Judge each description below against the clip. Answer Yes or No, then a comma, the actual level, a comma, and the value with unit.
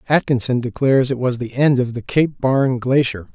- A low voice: Yes, low, 130 Hz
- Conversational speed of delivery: Yes, average, 195 wpm